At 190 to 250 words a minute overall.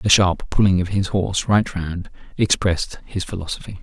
No: average, 175 wpm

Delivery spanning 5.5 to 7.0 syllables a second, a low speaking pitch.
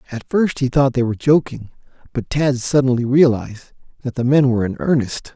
Yes: 5.9 syllables/s; low, 130 Hz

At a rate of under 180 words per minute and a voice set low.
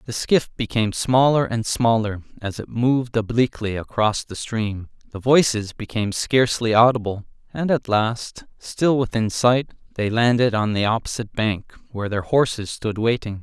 Yes: average, 155 wpm; low, 115 Hz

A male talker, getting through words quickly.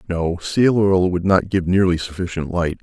No: male; average, 190 wpm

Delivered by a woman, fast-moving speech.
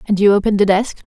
Yes: female; fast, 270 wpm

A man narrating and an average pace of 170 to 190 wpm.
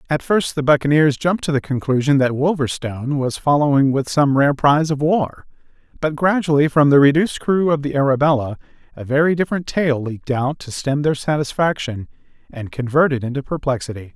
Yes: male; average, 180 wpm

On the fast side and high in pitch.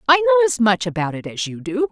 Yes: fast, 280 wpm; high, 240 Hz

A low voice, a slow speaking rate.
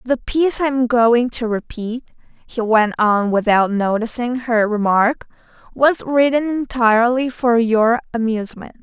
No: high, 235 Hz; slow, 130 wpm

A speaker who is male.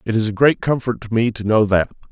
Yes: male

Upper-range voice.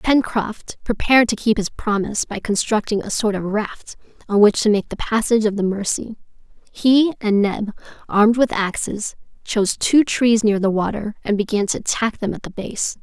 Yes: high, 215 Hz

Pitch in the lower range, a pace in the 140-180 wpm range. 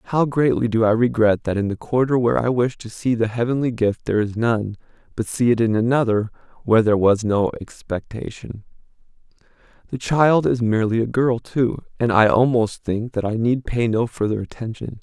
No: low, 115 Hz; average, 190 wpm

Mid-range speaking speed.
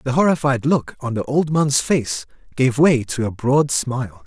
Yes: average, 195 wpm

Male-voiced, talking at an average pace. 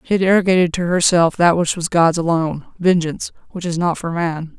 No: female; average, 195 wpm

